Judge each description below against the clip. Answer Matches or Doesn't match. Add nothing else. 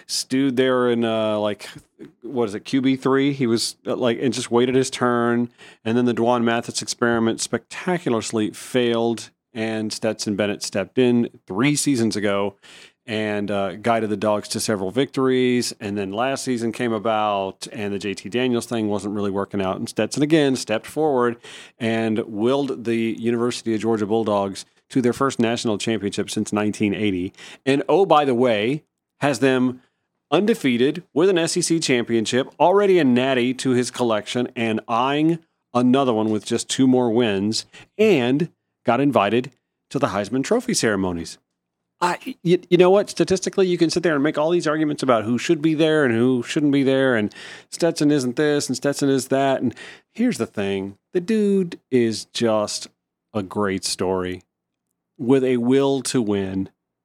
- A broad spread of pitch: Doesn't match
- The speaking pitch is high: Doesn't match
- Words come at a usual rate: Matches